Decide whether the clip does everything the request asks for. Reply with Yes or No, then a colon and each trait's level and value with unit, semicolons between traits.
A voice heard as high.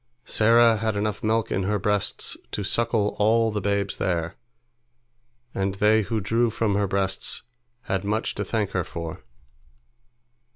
No: low, 105 Hz